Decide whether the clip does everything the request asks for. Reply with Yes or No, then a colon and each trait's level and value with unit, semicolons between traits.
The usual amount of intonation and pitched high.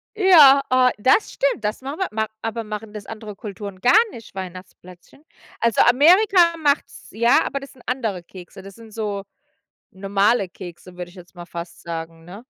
No: wide, 5.9 semitones; high, 215 Hz